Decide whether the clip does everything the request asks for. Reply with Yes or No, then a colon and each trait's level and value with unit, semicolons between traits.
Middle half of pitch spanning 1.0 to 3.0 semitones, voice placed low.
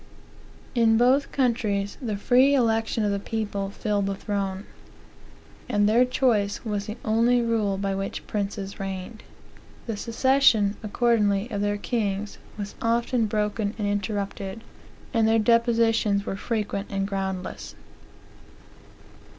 No: narrow, 2.5 semitones; high, 210 Hz